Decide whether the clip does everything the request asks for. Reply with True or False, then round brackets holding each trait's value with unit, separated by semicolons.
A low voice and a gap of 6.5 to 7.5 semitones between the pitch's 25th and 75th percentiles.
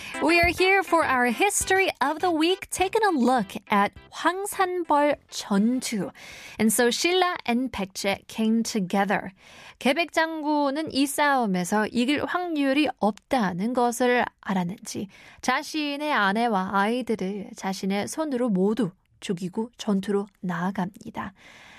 False (245 Hz; 7.0 semitones)